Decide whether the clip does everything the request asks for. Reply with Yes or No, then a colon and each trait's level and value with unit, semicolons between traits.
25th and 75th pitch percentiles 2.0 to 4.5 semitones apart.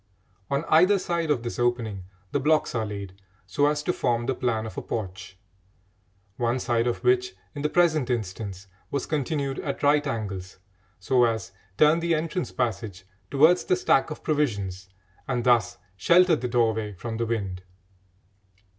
No: wide, 5.5 semitones